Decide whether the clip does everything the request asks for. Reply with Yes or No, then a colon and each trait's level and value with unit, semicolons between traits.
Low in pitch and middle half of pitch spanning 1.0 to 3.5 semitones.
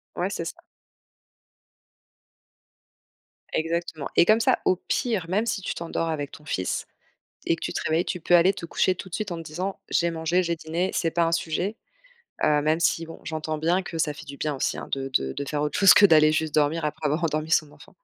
No: medium, 165 Hz; narrow, 2.4 semitones